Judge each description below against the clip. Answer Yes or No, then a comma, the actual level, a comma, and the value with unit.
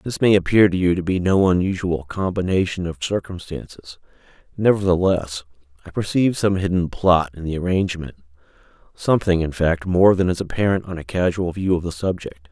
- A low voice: Yes, very low, 90 Hz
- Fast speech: No, average, 165 wpm